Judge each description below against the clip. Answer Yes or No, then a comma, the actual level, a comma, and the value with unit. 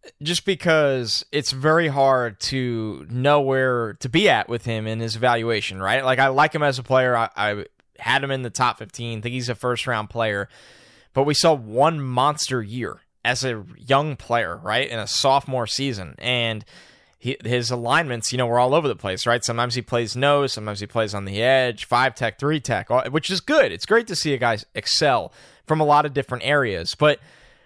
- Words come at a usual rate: No, fast, 210 wpm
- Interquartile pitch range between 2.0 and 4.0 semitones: Yes, average, 3.5 semitones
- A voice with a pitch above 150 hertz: No, low, 125 Hz